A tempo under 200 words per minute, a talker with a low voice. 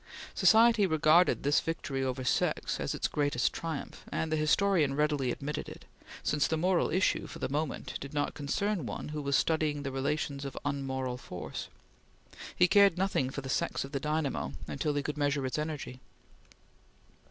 No: average, 175 wpm; medium, 150 Hz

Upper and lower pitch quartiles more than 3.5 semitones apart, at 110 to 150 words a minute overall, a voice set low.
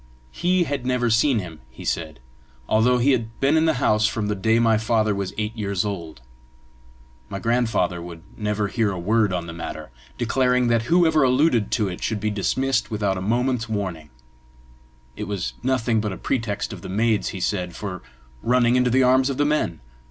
No: average, 4.1 semitones; average, 195 wpm; low, 110 Hz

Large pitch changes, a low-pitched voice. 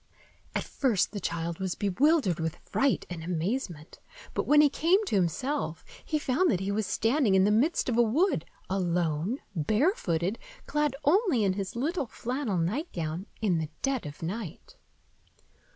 No: wide, 8.0 semitones; high, 210 Hz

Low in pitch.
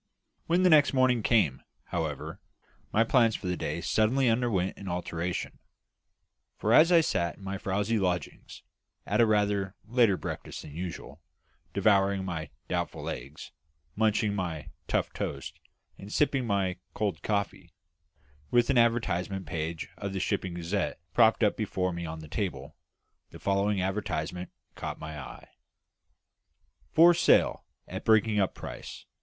Yes: low, 100 Hz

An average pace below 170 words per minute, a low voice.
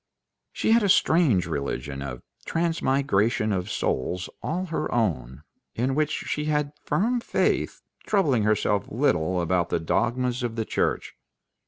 Yes: average, 140 wpm; low, 115 Hz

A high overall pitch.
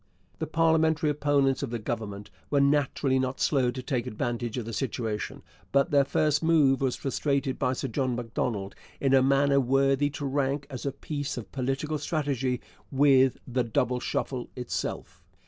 No: low, 135 Hz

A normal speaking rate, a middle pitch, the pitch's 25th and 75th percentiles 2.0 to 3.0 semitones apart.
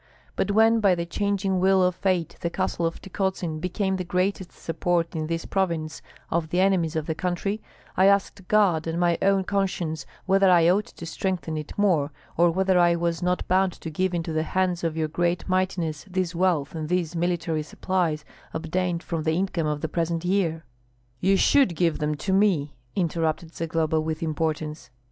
Yes: average, 185 wpm; medium, 175 Hz; average, 2.7 semitones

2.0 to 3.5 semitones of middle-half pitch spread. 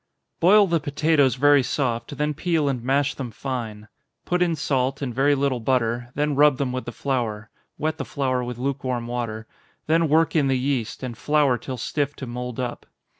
Yes: average, 3.0 semitones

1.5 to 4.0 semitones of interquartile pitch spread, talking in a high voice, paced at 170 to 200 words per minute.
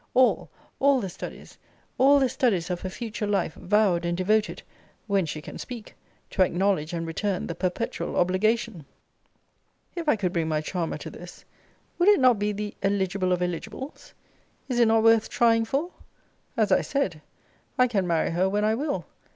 No: average, 4.7 semitones; high, 205 Hz; average, 175 wpm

